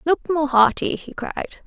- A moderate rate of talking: Yes, average, 180 wpm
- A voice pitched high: Yes, very high, 300 Hz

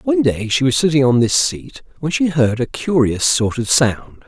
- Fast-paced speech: Yes, fast, 225 wpm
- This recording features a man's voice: Yes, male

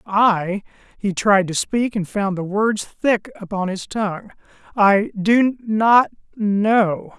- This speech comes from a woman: No, male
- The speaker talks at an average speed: No, slow, 125 wpm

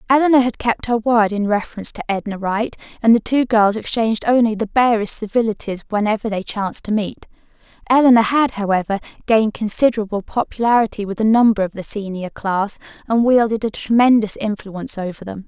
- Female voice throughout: Yes, female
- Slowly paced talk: No, average, 170 wpm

